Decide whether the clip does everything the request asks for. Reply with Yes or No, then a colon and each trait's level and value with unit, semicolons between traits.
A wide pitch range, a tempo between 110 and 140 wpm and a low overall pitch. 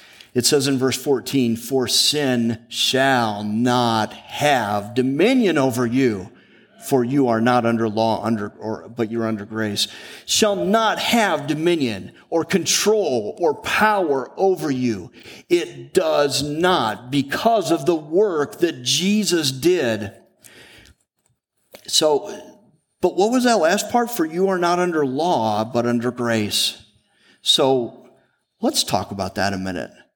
Yes: wide, 7.4 semitones; slow, 135 wpm; low, 130 Hz